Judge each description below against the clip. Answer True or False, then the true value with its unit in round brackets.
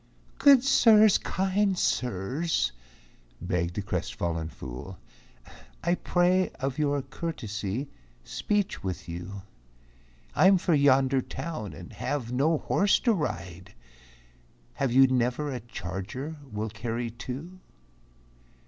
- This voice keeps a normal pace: False (110 wpm)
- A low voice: True (130 Hz)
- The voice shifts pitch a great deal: True (9.0 semitones)